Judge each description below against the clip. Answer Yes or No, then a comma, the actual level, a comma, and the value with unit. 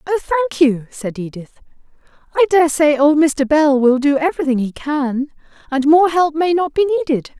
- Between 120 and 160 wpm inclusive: No, average, 185 wpm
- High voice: Yes, very high, 295 Hz